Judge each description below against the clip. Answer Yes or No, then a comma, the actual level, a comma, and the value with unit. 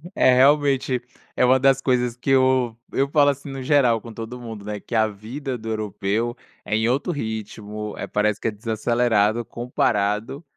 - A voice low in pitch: Yes, low, 120 Hz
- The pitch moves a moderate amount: Yes, average, 3.3 semitones